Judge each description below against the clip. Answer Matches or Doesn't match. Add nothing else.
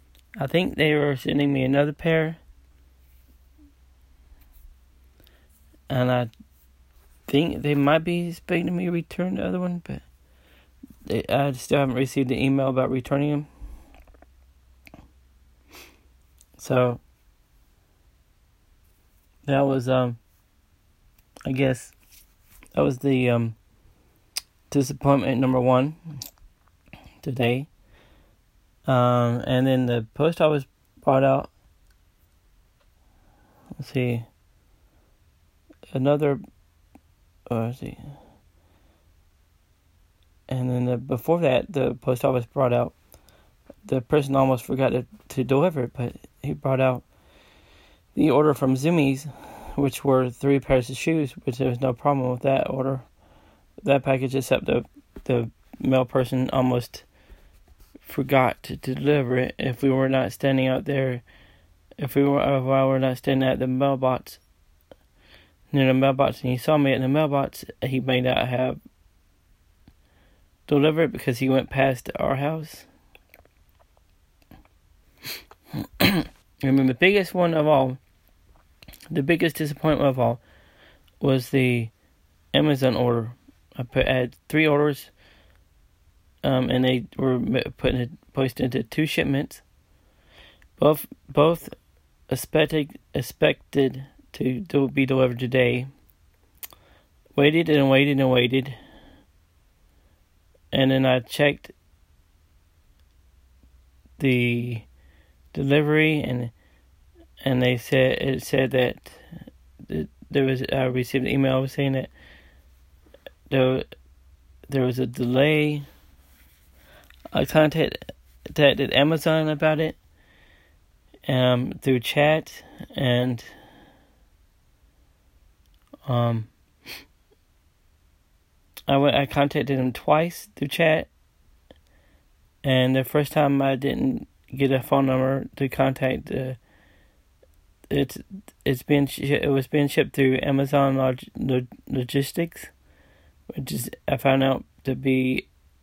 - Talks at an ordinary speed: Doesn't match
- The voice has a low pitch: Matches